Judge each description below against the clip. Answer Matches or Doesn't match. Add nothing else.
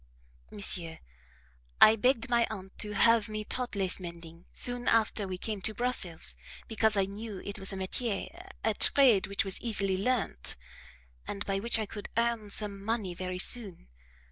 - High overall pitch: Matches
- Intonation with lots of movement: Doesn't match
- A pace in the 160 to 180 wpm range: Matches